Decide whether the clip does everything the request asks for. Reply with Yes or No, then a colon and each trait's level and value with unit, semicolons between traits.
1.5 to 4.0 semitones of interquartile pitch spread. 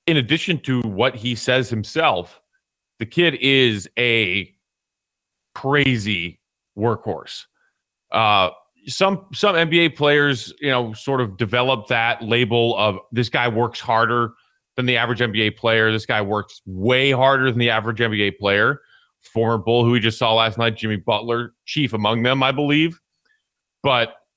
Yes: average, 3.3 semitones